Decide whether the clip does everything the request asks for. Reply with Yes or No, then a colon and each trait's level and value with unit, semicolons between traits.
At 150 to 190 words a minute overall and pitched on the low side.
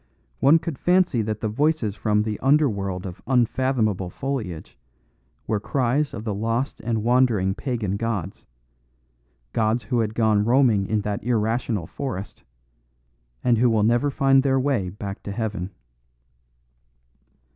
No: average, 140 wpm; low, 115 Hz